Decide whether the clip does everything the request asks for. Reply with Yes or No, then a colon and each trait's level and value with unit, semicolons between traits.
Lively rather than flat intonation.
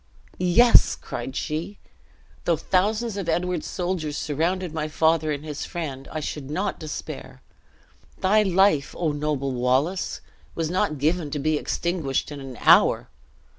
No: average, 3.6 semitones